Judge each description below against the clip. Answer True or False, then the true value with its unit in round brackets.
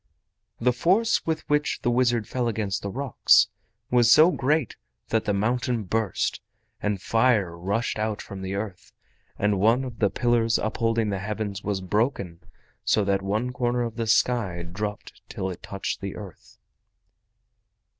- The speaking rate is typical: True (155 wpm)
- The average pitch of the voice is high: False (110 Hz)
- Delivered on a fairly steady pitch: False (3.6 semitones)